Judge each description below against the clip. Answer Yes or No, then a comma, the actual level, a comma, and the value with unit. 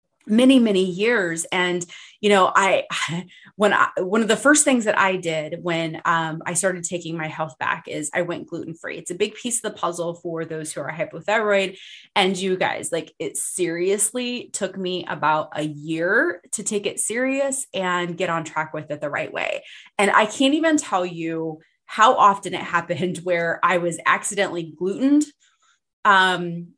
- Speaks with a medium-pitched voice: Yes, medium, 180 Hz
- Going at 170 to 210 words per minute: Yes, average, 180 wpm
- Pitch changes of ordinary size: Yes, average, 3.9 semitones